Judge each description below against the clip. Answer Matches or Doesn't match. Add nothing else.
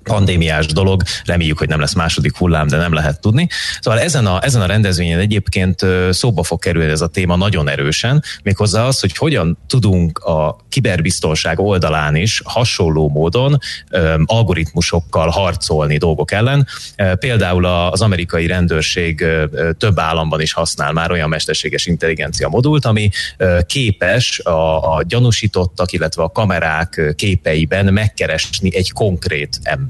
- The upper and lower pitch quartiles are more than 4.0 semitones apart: Matches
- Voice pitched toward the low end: Matches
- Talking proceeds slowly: Doesn't match